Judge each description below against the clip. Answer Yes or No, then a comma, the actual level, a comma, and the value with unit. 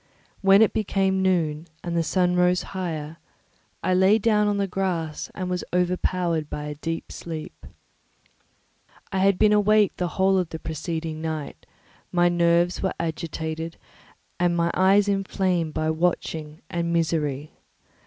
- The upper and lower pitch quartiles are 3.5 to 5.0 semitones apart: No, average, 2.8 semitones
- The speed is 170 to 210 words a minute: No, average, 145 wpm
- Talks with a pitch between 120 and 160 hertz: No, medium, 175 Hz